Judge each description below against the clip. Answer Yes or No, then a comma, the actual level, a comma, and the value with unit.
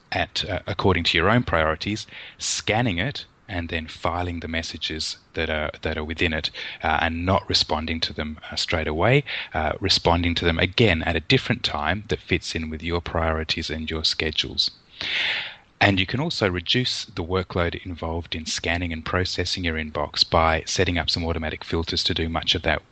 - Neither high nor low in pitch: No, very low, 85 Hz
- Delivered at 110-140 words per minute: No, average, 190 wpm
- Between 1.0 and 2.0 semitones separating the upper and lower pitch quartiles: No, average, 2.9 semitones